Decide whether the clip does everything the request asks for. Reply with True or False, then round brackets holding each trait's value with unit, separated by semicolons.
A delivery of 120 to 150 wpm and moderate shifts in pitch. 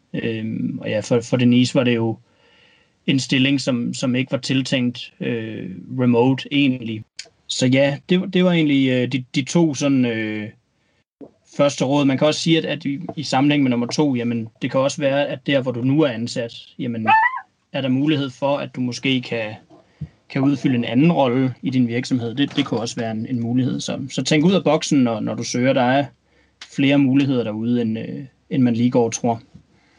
False (210 wpm; 3.0 semitones)